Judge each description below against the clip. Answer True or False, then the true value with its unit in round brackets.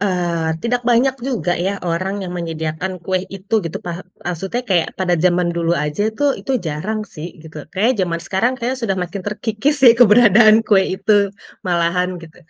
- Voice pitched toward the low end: False (190 Hz)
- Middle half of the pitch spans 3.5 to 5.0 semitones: True (4.2 semitones)